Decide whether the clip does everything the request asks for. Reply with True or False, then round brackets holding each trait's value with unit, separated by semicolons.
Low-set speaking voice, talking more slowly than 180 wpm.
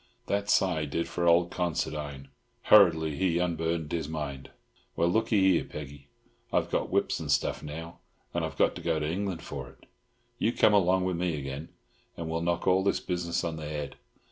False (85 Hz; 185 wpm)